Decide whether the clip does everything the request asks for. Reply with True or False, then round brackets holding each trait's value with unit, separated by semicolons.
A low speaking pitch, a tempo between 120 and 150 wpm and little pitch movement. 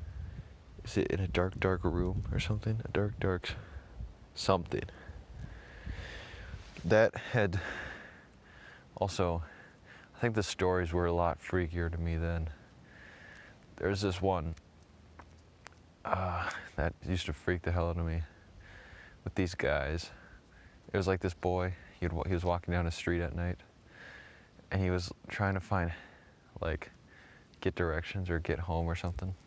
True (90 Hz; 140 wpm; 2.1 semitones)